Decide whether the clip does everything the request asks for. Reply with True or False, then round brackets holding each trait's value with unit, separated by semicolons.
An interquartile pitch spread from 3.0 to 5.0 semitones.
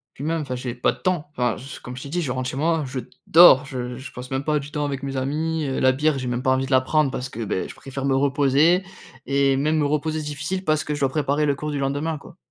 False (2.6 semitones)